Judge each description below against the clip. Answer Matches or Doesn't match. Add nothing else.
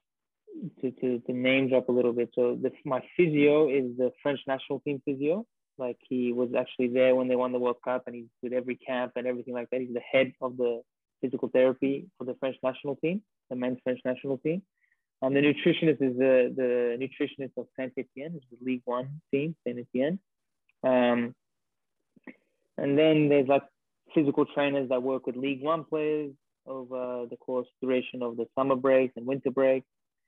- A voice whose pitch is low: Matches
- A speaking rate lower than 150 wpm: Doesn't match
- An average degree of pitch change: Doesn't match